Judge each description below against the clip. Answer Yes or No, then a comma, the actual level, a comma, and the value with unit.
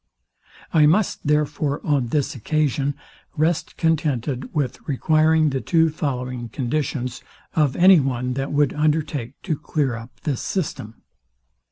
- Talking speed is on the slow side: Yes, slow, 130 wpm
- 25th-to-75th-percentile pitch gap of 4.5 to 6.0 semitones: No, average, 3.4 semitones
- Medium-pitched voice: Yes, medium, 145 Hz